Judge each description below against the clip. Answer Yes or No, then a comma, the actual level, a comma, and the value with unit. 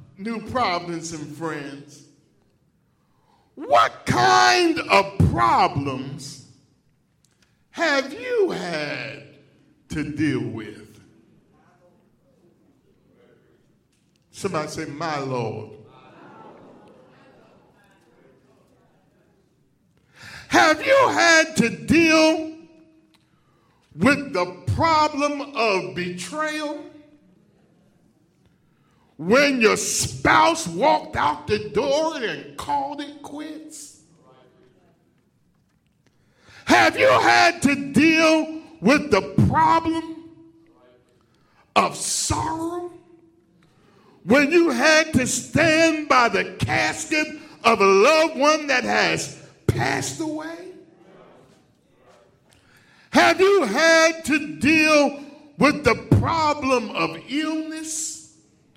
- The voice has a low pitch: No, very high, 285 Hz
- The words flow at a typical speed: No, slow, 75 wpm